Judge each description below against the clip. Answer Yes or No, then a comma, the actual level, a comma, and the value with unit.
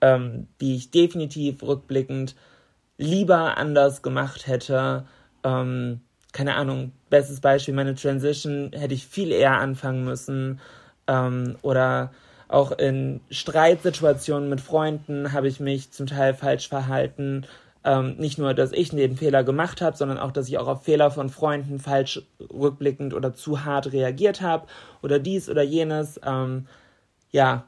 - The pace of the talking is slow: No, average, 145 wpm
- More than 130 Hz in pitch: Yes, medium, 140 Hz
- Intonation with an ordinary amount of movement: No, narrow, 1.8 semitones